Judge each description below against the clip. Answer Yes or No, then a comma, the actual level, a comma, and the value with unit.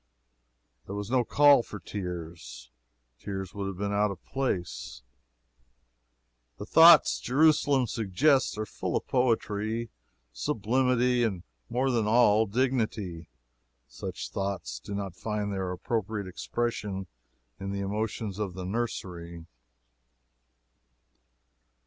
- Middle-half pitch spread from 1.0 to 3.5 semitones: No, average, 4.0 semitones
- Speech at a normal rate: No, slow, 110 wpm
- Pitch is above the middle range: No, low, 105 Hz